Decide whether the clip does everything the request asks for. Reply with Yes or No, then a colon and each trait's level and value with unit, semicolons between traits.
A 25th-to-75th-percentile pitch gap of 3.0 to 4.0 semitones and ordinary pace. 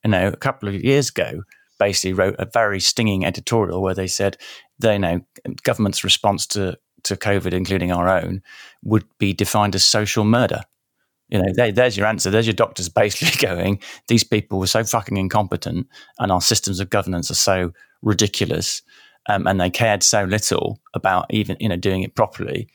No: narrow, 2.5 semitones; average, 185 wpm